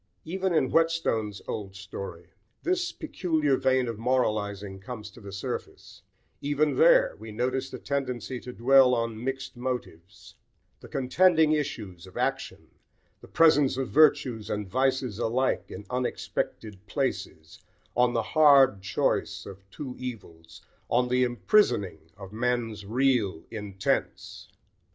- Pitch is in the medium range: No, low, 125 Hz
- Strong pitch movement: No, average, 4.8 semitones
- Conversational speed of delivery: No, slow, 130 wpm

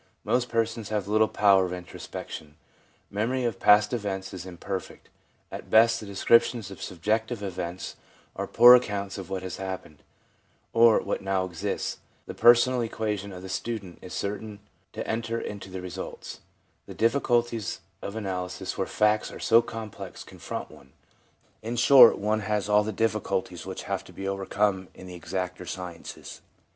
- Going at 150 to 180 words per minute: Yes, average, 165 wpm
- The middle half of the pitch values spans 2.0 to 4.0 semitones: Yes, average, 3.2 semitones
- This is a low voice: Yes, low, 100 Hz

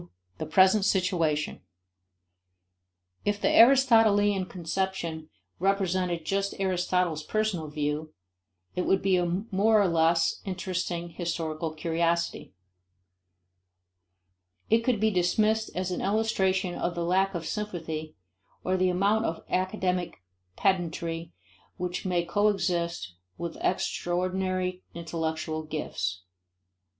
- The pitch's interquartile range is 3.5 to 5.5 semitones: No, average, 2.7 semitones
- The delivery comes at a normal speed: No, slow, 105 wpm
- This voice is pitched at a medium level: Yes, medium, 180 Hz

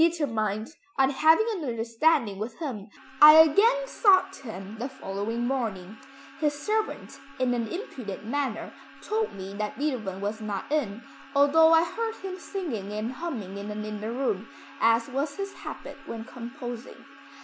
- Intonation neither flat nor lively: No, wide, 6.8 semitones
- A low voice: No, very high, 250 Hz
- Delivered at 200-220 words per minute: No, average, 150 wpm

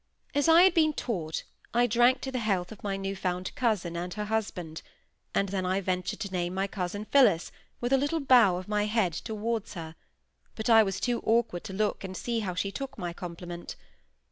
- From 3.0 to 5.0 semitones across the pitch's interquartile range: Yes, average, 4.5 semitones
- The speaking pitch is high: Yes, high, 205 Hz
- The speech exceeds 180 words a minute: Yes, fast, 205 wpm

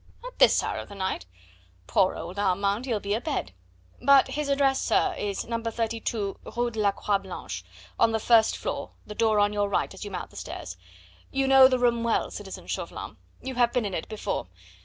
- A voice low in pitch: No, high, 220 Hz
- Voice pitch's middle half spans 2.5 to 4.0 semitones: Yes, average, 3.3 semitones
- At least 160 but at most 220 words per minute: Yes, fast, 205 wpm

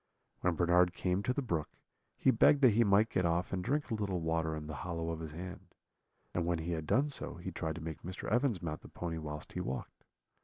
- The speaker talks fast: Yes, fast, 240 wpm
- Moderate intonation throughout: Yes, average, 3.5 semitones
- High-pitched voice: No, very low, 85 Hz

